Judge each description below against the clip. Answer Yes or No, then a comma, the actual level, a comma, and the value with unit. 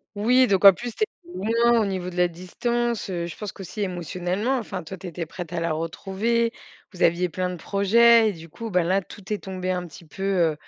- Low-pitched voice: No, high, 190 Hz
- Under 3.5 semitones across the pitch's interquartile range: No, average, 3.8 semitones